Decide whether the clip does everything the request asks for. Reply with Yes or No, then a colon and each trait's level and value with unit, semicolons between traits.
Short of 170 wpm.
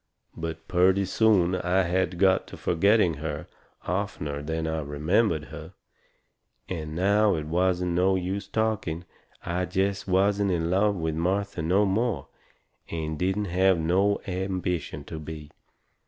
Yes: average, 140 wpm